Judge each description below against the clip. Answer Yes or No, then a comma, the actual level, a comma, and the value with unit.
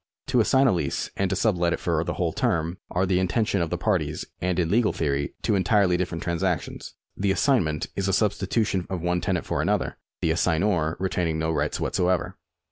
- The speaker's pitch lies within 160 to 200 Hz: No, very low, 90 Hz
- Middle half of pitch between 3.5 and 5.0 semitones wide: No, average, 2.8 semitones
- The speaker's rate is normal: No, fast, 210 wpm